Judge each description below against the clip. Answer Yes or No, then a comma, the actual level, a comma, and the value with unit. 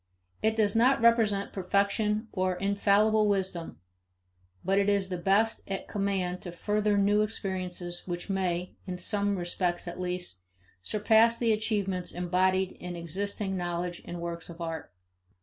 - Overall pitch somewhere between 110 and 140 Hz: No, high, 190 Hz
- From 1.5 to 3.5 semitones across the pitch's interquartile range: Yes, average, 2.7 semitones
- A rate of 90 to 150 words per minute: Yes, average, 145 wpm